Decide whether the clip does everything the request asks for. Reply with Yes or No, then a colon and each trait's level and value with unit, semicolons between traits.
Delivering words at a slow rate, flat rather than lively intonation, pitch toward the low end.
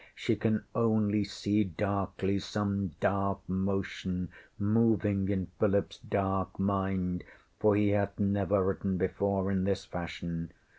Yes: slow, 120 wpm; narrow, 1.3 semitones; low, 100 Hz